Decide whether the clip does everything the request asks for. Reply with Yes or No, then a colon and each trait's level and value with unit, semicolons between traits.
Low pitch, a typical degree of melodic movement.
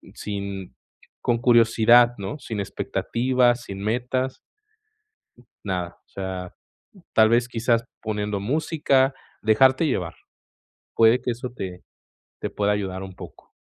Yes: low, 115 Hz; average, 3.7 semitones